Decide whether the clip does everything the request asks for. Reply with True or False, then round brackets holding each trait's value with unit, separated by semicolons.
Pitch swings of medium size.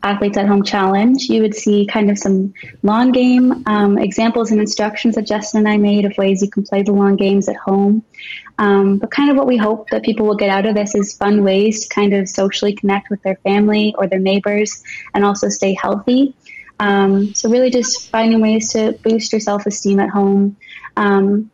False (1.8 semitones)